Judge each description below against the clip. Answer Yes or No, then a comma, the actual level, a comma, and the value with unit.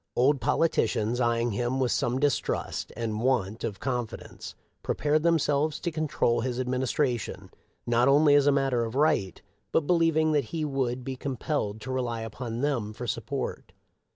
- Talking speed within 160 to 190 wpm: Yes, average, 170 wpm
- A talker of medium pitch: No, low, 130 Hz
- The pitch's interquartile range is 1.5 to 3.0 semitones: No, average, 3.6 semitones